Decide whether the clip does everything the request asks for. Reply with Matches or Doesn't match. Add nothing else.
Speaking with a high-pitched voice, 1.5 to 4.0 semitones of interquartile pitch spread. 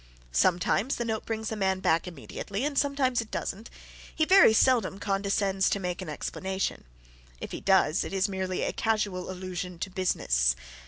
Matches